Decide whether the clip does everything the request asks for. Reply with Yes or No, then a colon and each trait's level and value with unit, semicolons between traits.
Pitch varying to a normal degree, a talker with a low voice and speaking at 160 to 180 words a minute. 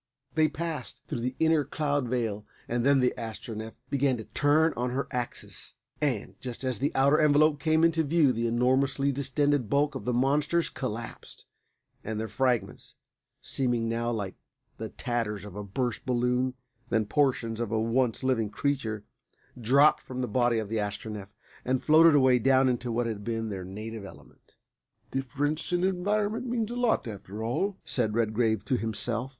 Yes: average, 4.2 semitones; low, 125 Hz; average, 170 wpm